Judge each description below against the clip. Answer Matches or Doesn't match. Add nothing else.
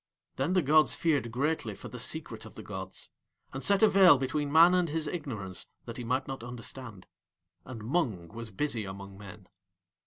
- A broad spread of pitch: Matches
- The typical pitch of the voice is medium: Doesn't match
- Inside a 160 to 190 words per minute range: Matches